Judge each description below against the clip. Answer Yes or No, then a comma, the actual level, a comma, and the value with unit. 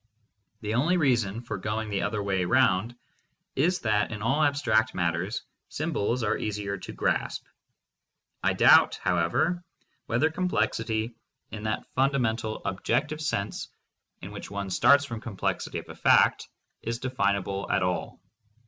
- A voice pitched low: Yes, low, 110 Hz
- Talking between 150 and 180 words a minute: No, average, 140 wpm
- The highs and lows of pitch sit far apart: No, average, 4.8 semitones